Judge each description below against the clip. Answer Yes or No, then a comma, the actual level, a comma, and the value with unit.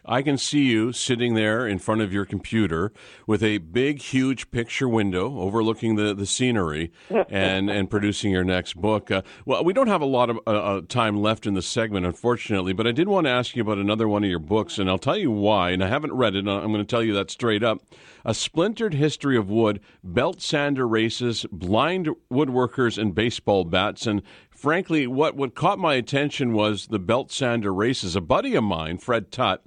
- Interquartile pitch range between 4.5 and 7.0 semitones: No, average, 4.1 semitones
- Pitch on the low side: Yes, low, 110 Hz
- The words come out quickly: Yes, fast, 210 wpm